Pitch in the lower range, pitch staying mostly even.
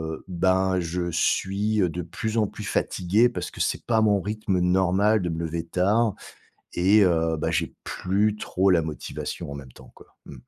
No: very low, 95 Hz; average, 3.6 semitones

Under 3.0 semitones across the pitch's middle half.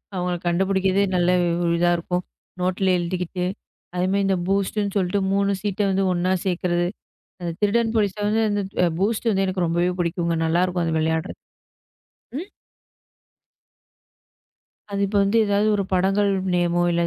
Yes: narrow, 2.4 semitones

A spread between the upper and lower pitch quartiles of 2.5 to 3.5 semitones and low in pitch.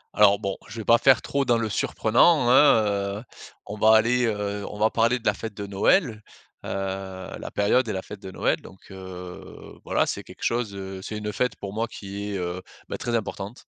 Yes: average, 2.9 semitones; low, 105 Hz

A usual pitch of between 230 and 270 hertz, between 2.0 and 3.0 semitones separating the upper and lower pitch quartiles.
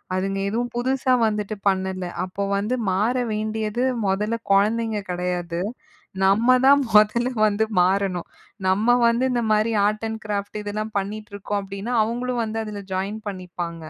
No: high, 210 Hz; narrow, 2.6 semitones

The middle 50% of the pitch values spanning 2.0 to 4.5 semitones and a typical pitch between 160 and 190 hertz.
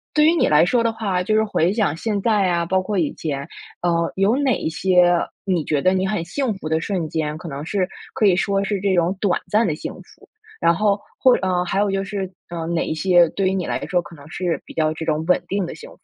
Yes: average, 3.3 semitones; medium, 185 Hz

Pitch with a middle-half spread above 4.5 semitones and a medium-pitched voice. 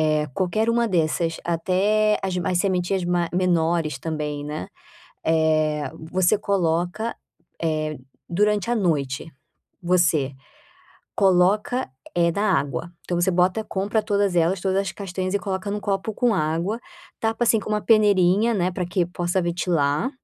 No: average, 3.6 semitones; medium, 180 Hz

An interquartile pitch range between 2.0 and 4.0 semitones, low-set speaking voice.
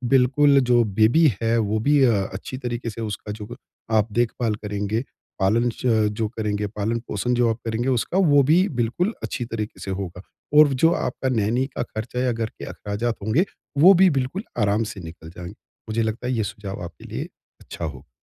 Yes: average, 3.2 semitones; low, 115 Hz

